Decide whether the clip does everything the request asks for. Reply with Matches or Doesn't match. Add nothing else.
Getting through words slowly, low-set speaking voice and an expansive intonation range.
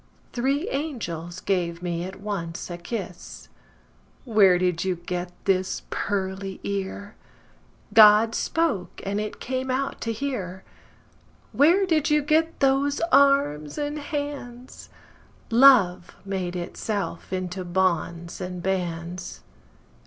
Doesn't match